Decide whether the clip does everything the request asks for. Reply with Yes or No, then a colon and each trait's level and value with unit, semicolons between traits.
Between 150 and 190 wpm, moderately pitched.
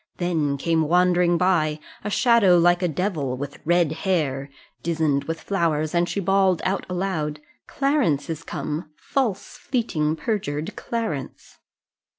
No: slow, 135 wpm; medium, 170 Hz